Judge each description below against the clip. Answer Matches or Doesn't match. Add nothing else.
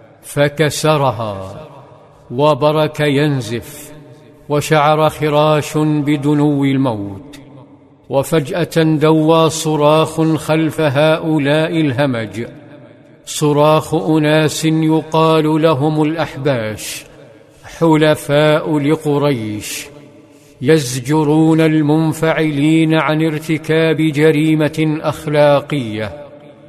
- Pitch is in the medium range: Matches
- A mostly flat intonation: Matches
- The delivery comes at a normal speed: Doesn't match